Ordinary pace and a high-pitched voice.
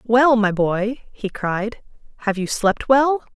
Yes: average, 160 wpm; high, 225 Hz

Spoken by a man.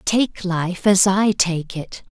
No: female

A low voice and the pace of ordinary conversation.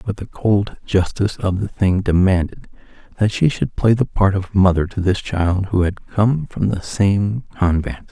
Yes: low, 100 Hz; average, 190 wpm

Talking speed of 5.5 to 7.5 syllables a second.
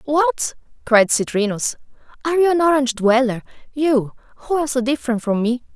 Yes: 5.8 syllables/s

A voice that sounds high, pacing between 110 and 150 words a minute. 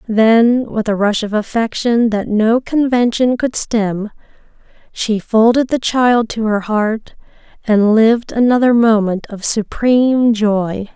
Yes: high, 225 Hz; slow, 135 wpm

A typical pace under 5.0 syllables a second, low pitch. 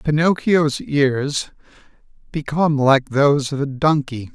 No: 4.0 syllables/s; medium, 145 Hz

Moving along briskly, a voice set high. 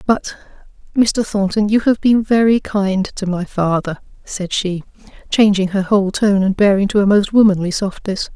No: average, 170 wpm; high, 200 Hz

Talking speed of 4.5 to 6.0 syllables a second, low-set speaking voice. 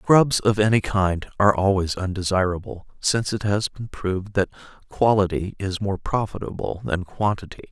Yes: 5.0 syllables/s; low, 100 Hz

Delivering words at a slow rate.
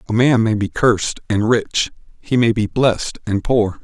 No: fast, 205 wpm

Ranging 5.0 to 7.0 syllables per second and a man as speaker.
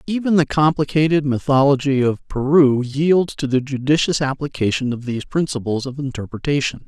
Yes: 5.4 syllables/s; male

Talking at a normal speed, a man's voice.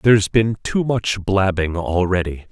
Yes: average, 145 wpm; male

